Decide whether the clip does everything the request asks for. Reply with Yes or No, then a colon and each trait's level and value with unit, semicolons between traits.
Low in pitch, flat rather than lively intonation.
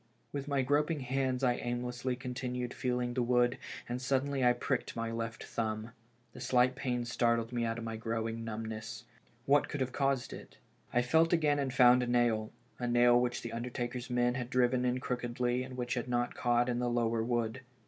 Yes: low, 125 Hz; narrow, 1.2 semitones